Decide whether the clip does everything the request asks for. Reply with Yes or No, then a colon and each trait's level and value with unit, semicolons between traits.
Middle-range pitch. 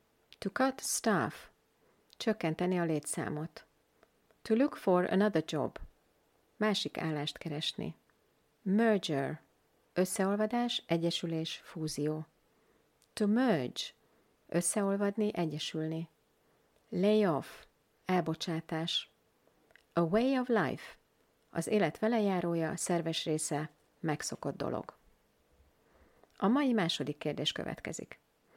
Yes: medium, 170 Hz